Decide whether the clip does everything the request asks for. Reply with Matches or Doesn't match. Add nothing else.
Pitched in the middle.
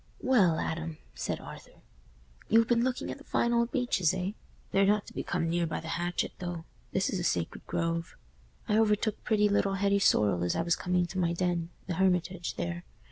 Matches